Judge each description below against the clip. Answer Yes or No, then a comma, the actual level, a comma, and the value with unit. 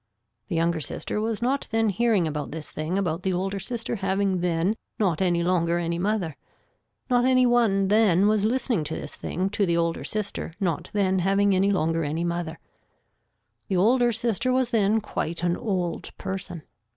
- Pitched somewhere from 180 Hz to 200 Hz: Yes, high, 190 Hz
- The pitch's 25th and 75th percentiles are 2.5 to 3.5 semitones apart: No, average, 4.1 semitones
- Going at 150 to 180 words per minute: Yes, average, 175 wpm